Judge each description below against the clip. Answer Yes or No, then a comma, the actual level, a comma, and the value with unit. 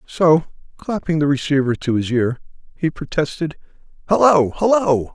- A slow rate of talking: Yes, slow, 130 wpm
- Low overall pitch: No, medium, 155 Hz